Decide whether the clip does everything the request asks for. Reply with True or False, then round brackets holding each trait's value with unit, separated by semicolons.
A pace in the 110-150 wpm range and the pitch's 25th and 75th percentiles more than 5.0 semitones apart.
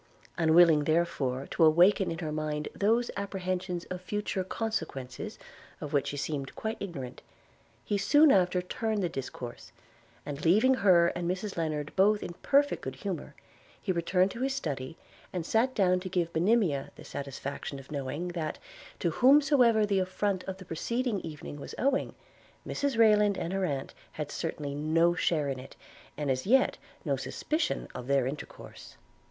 False (165 wpm; 5.5 semitones)